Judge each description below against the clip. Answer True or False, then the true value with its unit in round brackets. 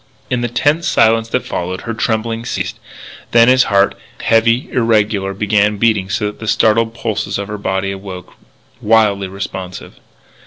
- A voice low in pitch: True (110 Hz)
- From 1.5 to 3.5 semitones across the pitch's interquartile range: True (2.6 semitones)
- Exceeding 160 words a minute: False (155 wpm)